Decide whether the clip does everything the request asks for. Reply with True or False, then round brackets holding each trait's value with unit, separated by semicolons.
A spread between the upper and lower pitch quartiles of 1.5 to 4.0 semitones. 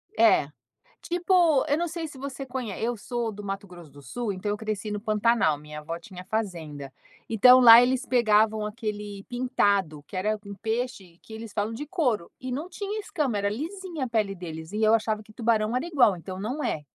False (4.4 semitones)